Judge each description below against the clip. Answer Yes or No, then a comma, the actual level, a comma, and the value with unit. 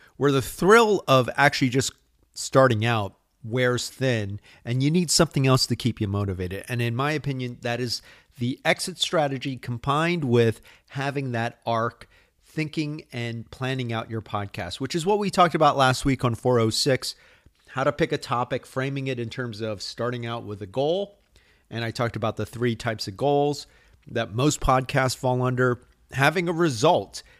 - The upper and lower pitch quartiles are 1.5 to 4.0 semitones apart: Yes, average, 3.4 semitones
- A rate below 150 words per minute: No, average, 175 wpm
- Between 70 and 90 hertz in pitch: No, low, 125 Hz